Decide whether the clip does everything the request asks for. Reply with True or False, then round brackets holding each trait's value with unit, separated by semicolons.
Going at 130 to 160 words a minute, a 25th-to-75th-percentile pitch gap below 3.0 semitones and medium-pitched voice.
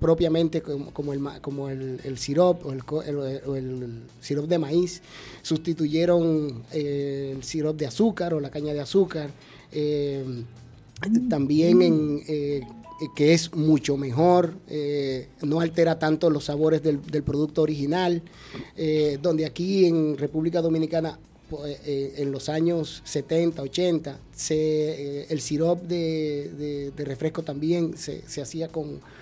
True (140 wpm; 2.5 semitones; 155 Hz)